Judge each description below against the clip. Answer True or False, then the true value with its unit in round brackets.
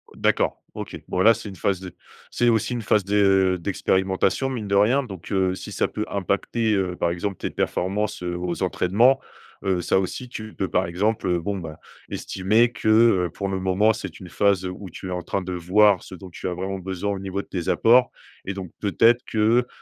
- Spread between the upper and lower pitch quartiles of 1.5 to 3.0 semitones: True (2.7 semitones)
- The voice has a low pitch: True (95 Hz)